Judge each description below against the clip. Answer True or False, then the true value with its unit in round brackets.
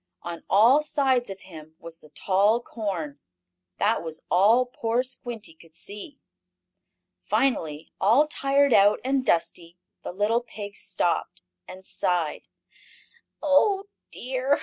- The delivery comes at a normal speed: False (125 wpm)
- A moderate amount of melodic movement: False (6.9 semitones)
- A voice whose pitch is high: True (210 Hz)